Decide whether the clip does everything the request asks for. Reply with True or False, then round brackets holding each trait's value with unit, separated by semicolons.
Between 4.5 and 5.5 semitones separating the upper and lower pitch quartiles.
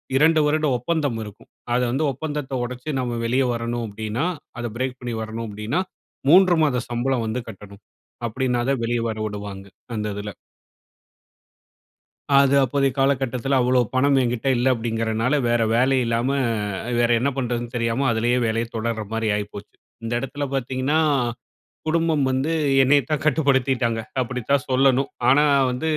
False (3.0 semitones)